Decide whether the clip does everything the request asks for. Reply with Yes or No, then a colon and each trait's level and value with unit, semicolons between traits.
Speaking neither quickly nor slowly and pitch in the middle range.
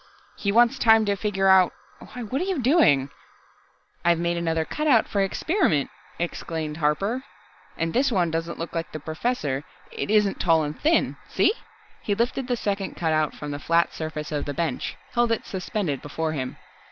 Yes: average, 175 wpm; medium, 175 Hz